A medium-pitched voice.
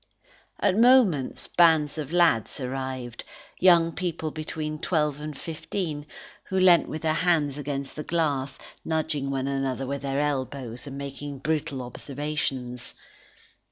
Yes: medium, 150 Hz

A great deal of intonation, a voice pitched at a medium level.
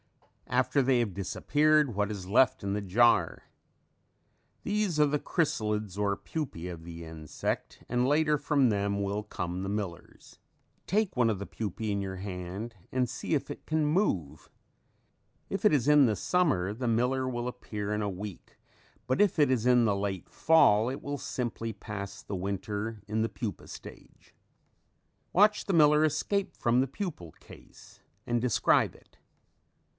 No: wide, 6.1 semitones; low, 115 Hz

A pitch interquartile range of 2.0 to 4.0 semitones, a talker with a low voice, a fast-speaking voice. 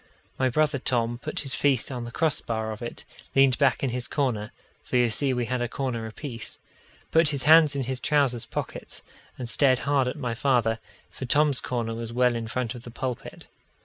Yes: average, 2.8 semitones; low, 125 Hz; fast, 210 wpm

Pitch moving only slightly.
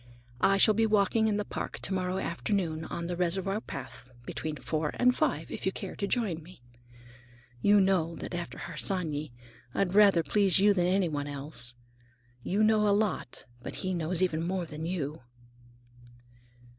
No: average, 3.9 semitones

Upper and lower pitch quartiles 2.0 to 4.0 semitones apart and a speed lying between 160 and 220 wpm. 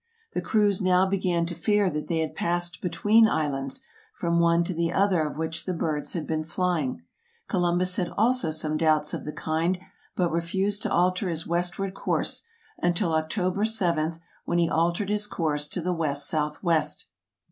Yes: average, 2.7 semitones; average, 180 wpm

